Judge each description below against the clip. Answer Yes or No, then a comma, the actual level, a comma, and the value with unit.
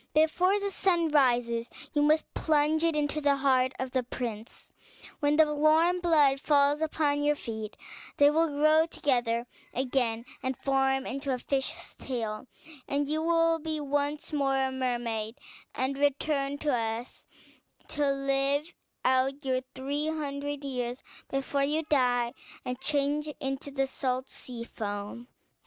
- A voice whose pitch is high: Yes, very high, 275 Hz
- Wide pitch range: No, average, 2.8 semitones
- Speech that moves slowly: No, average, 145 wpm